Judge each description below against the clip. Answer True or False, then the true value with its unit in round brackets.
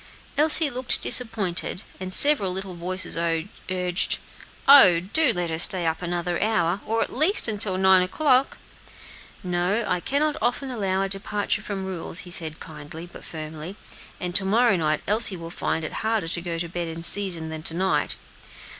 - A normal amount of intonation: True (4.2 semitones)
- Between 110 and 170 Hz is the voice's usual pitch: False (185 Hz)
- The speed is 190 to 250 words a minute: False (170 wpm)